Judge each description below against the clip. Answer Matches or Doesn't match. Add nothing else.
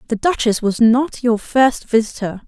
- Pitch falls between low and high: Doesn't match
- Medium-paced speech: Matches